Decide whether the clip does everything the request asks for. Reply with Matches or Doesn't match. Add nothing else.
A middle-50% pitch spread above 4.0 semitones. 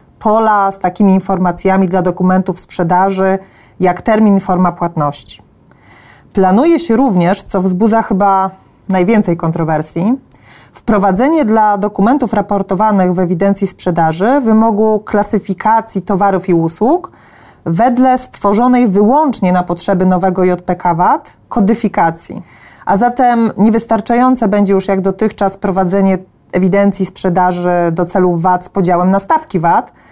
Doesn't match